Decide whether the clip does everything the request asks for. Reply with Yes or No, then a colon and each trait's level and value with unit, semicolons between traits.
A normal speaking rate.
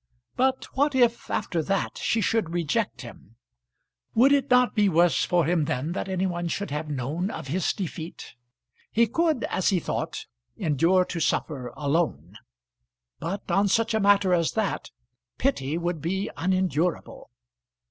Yes: average, 155 wpm